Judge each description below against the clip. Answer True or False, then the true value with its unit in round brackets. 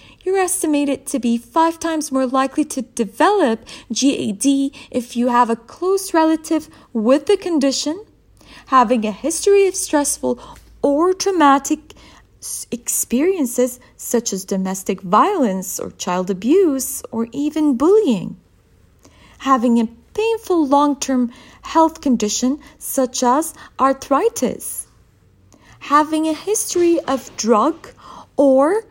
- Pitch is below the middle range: False (280 Hz)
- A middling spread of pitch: True (4.7 semitones)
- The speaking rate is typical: False (110 wpm)